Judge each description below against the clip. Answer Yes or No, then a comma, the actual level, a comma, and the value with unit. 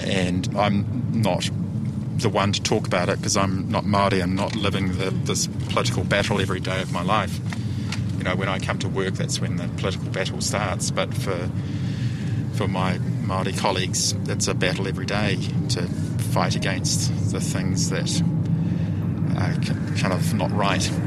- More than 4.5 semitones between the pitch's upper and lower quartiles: Yes, average, 5.0 semitones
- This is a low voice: Yes, low, 105 Hz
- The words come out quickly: No, average, 170 wpm